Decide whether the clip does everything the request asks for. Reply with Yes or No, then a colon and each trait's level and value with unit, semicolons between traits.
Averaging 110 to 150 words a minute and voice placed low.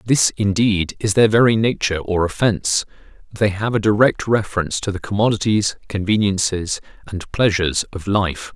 Yes: average, 145 wpm; low, 100 Hz